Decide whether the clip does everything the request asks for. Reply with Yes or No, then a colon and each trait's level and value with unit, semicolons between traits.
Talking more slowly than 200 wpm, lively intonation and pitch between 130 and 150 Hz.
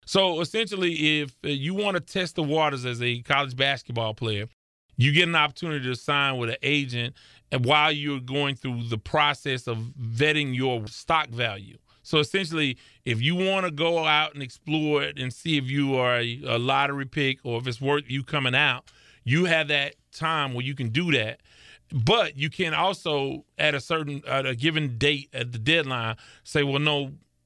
No: average, 190 wpm; average, 3.7 semitones; medium, 140 Hz